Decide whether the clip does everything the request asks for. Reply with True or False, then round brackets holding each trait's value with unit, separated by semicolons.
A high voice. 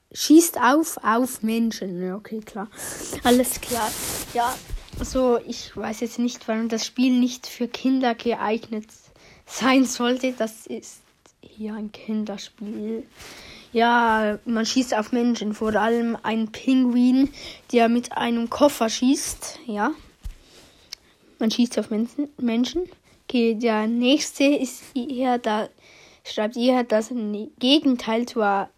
True (235 Hz)